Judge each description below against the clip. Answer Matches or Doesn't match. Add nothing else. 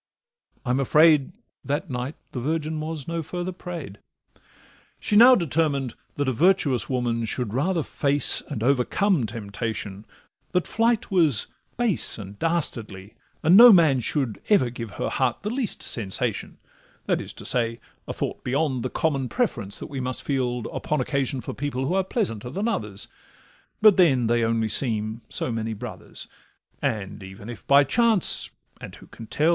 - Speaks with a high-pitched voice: Doesn't match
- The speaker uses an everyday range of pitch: Doesn't match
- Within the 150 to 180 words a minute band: Matches